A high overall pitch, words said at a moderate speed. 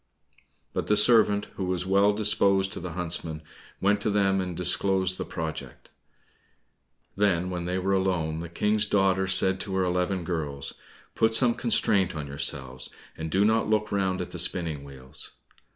No: very low, 95 Hz; average, 170 wpm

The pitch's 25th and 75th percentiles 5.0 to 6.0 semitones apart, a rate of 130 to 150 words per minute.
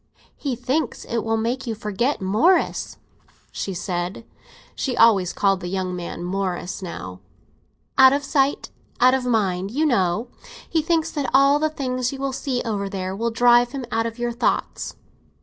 No: wide, 5.5 semitones; average, 170 wpm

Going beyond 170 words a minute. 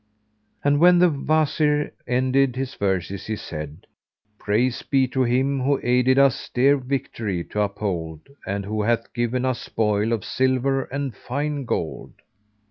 No: average, 145 wpm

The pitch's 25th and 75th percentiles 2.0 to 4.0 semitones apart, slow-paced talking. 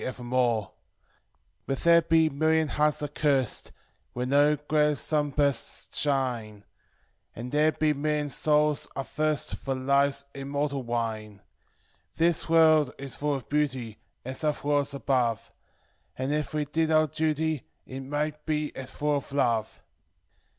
Yes: narrow, 2.6 semitones; slow, 130 wpm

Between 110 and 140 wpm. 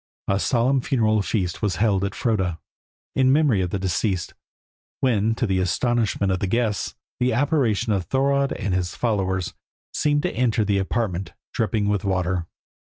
No: average, 165 wpm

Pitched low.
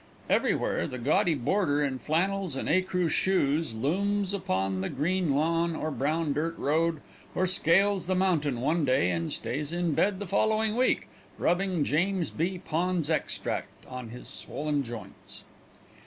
No: medium, 165 Hz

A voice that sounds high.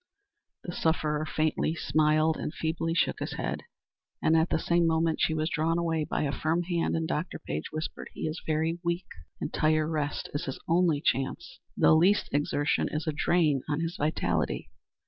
No: medium, 160 Hz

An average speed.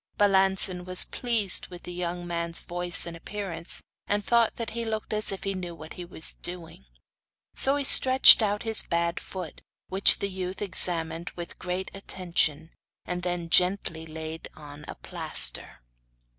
Yes: average, 160 wpm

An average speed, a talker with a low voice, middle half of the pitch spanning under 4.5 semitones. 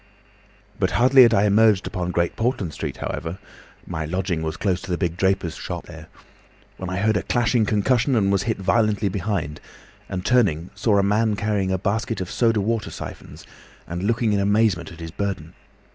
Yes: average, 190 wpm; low, 100 Hz; average, 3.6 semitones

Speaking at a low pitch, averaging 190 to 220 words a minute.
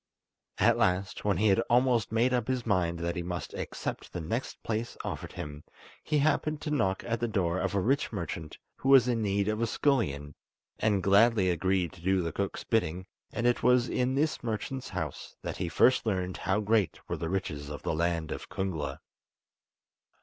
Yes: low, 100 Hz; average, 195 wpm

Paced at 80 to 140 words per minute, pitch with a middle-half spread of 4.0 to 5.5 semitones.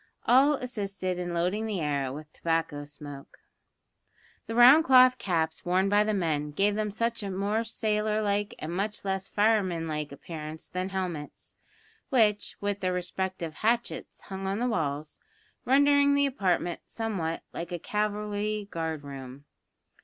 No: average, 155 wpm; average, 4.7 semitones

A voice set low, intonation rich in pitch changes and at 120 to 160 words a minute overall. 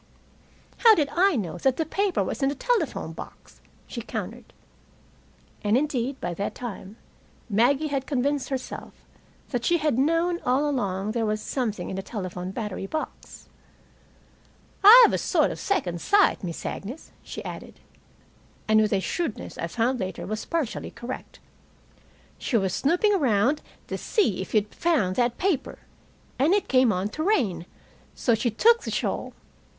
No: very high, 250 Hz; wide, 7.1 semitones; average, 155 wpm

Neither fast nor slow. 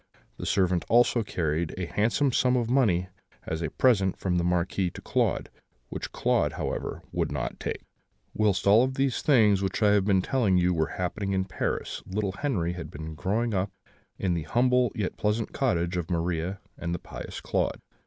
Yes: average, 185 wpm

